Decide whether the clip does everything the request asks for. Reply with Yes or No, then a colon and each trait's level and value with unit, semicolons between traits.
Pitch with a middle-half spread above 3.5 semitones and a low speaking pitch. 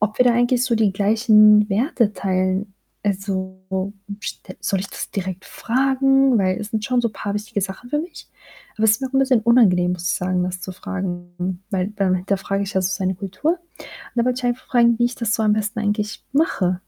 No: average, 4.1 semitones; high, 205 Hz